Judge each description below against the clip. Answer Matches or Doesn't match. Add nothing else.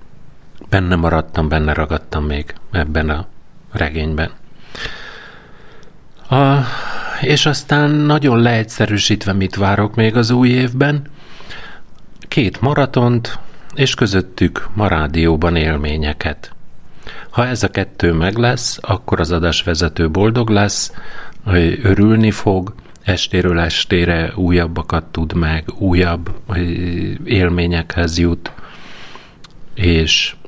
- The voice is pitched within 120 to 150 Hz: Doesn't match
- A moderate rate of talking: Doesn't match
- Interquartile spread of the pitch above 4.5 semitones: Matches